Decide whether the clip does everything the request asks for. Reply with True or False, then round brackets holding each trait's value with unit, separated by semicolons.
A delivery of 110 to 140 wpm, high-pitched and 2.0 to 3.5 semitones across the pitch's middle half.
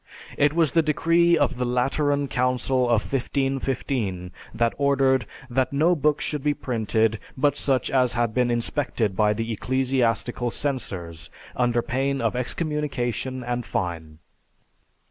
False (135 wpm; 125 Hz; 3.1 semitones)